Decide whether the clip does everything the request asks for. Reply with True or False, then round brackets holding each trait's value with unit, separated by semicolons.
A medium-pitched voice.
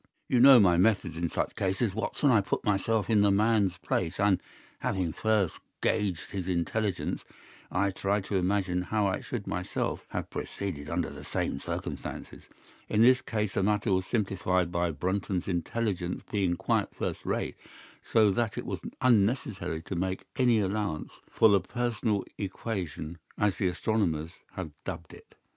False (100 Hz)